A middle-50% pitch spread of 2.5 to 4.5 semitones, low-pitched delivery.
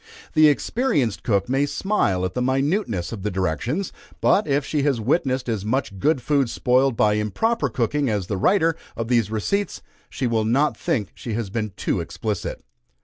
No: wide, 5.5 semitones; low, 125 Hz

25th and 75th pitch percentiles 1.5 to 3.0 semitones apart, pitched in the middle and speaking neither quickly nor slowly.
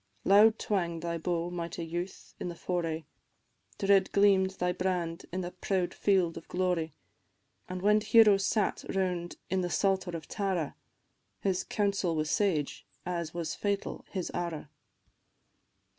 Yes: narrow, 2.4 semitones; medium, 180 Hz; average, 145 wpm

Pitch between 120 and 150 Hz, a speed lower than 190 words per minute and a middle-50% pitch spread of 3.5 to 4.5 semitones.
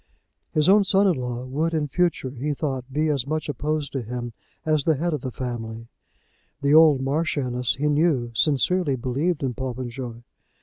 Yes: medium, 140 Hz; average, 175 wpm; average, 3.8 semitones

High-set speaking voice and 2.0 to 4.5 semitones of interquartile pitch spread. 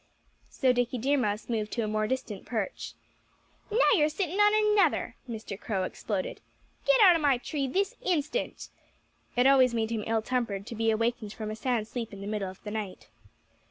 No: high, 235 Hz; average, 5.1 semitones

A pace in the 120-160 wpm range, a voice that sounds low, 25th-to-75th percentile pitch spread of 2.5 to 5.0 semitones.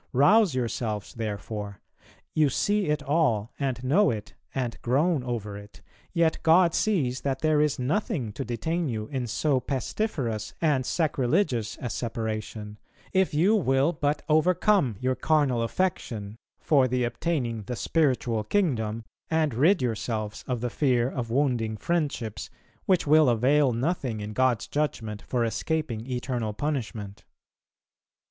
No: average, 140 wpm; low, 130 Hz; wide, 5.5 semitones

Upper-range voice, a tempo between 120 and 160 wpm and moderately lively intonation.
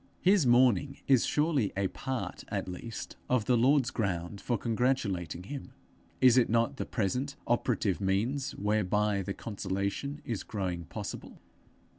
No: low, 115 Hz; average, 140 wpm; average, 4.9 semitones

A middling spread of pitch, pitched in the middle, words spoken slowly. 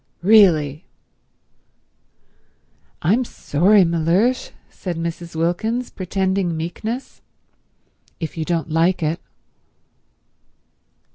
Yes: average, 3.6 semitones; medium, 175 Hz; slow, 75 wpm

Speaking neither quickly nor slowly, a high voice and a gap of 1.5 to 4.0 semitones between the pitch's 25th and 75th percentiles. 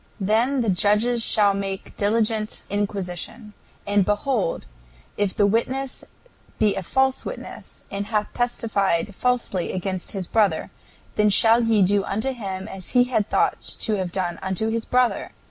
Yes: average, 150 wpm; high, 210 Hz; average, 2.9 semitones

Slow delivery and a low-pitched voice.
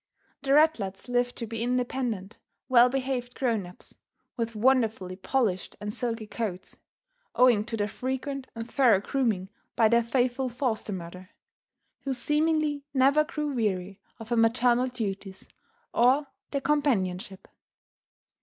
No: slow, 130 wpm; high, 240 Hz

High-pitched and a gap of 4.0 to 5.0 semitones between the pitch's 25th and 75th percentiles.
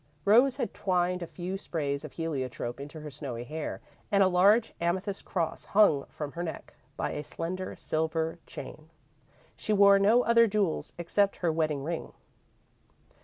No: medium, 170 Hz; average, 4.3 semitones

